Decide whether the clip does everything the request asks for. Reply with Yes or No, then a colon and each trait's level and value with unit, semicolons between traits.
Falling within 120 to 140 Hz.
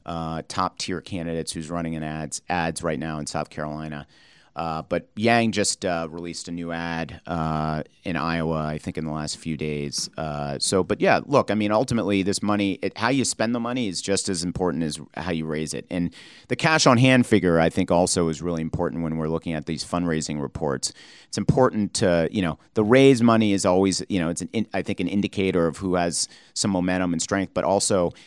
No: very low, 85 Hz